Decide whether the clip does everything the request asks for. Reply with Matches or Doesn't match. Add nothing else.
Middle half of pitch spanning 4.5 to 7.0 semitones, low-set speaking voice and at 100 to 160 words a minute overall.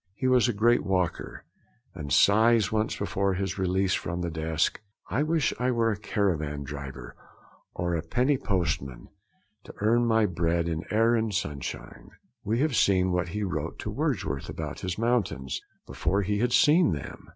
Doesn't match